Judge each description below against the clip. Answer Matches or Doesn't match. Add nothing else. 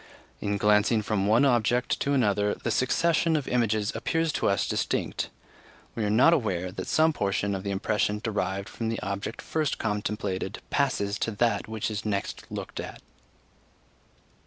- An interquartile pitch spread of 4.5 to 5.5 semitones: Doesn't match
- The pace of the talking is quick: Doesn't match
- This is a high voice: Doesn't match